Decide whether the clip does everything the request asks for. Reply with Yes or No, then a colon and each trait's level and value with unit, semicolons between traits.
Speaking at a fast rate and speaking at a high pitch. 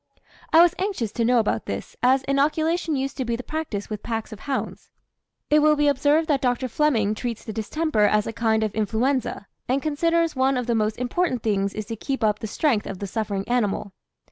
Yes: fast, 215 wpm; high, 245 Hz